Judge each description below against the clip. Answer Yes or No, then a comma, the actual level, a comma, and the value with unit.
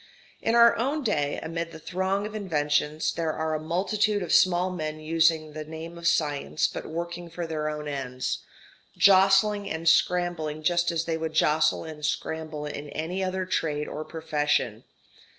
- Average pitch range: Yes, average, 3.0 semitones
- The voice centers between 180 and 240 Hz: No, medium, 160 Hz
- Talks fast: No, average, 170 wpm